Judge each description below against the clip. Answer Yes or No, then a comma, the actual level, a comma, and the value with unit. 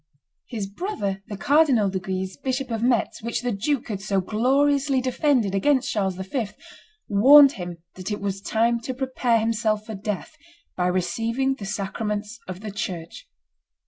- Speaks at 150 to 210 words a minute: Yes, average, 160 wpm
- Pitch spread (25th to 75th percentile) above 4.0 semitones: Yes, average, 4.8 semitones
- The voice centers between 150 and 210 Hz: No, high, 220 Hz